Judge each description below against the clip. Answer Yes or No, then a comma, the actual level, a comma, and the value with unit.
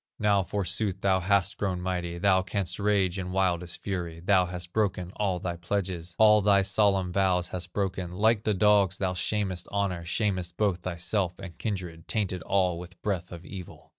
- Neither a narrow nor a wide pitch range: No, narrow, 2.1 semitones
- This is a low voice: Yes, very low, 95 Hz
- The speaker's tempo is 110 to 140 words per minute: No, average, 175 wpm